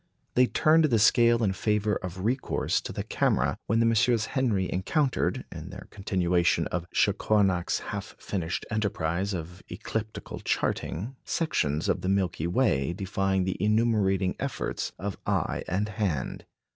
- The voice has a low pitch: Yes, low, 100 Hz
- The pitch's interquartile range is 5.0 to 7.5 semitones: No, average, 3.7 semitones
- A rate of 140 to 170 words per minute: Yes, average, 145 wpm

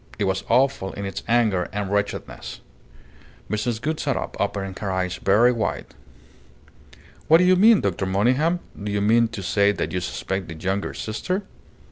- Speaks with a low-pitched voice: Yes, low, 105 Hz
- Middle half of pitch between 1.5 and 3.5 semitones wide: No, average, 4.3 semitones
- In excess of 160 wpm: Yes, average, 170 wpm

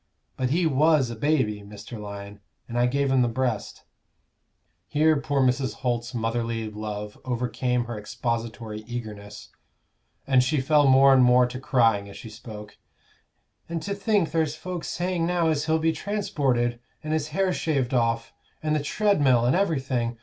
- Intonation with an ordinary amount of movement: Yes, average, 4.9 semitones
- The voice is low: Yes, low, 125 Hz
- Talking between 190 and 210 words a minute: No, average, 165 wpm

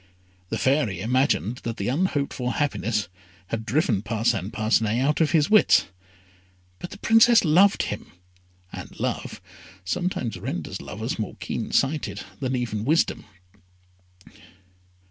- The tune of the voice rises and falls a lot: Yes, wide, 6.1 semitones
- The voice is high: No, low, 125 Hz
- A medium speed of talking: No, slow, 125 wpm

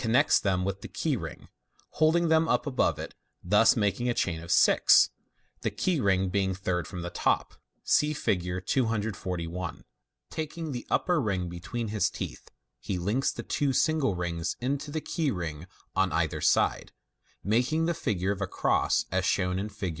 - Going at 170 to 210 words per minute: Yes, average, 175 wpm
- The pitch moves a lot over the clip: Yes, wide, 6.9 semitones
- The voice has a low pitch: Yes, low, 100 Hz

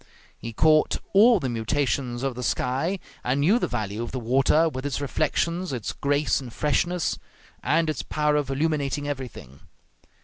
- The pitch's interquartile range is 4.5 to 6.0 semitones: No, average, 3.7 semitones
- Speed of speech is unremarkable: Yes, average, 165 wpm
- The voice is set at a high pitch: No, medium, 140 Hz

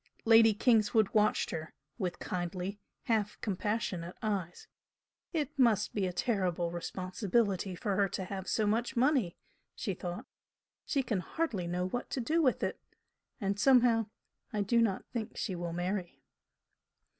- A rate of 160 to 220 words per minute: No, average, 145 wpm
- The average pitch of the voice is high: Yes, high, 205 Hz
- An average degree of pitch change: Yes, average, 4.1 semitones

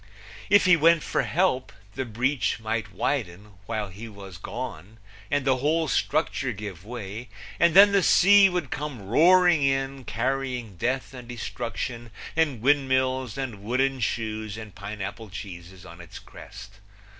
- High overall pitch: No, low, 125 Hz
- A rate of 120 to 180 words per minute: Yes, average, 145 wpm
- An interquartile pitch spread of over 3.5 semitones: Yes, average, 4.8 semitones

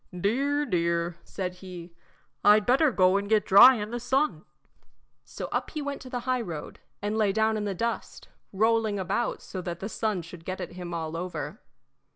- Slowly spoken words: No, average, 190 wpm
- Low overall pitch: No, high, 205 Hz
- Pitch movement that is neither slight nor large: Yes, average, 4.6 semitones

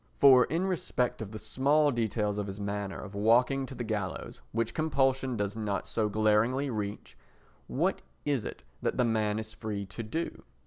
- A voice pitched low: Yes, low, 110 Hz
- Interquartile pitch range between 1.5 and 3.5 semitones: No, average, 4.0 semitones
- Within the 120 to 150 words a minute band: No, average, 180 wpm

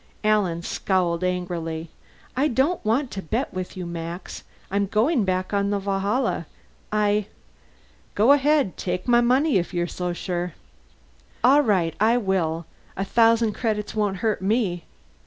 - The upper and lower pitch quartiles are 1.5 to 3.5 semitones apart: No, average, 4.4 semitones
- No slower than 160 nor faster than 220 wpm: No, average, 150 wpm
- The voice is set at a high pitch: Yes, high, 200 Hz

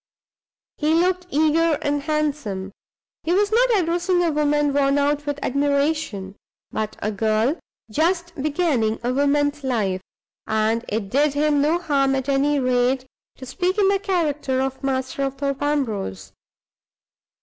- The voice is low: No, very high, 285 Hz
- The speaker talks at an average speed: Yes, average, 145 wpm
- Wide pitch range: No, average, 3.5 semitones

